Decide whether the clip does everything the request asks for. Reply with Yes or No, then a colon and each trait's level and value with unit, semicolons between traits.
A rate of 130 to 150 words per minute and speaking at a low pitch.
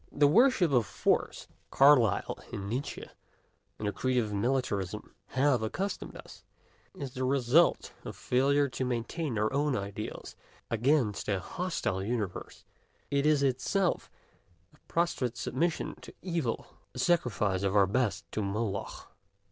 Yes: average, 140 wpm; low, 125 Hz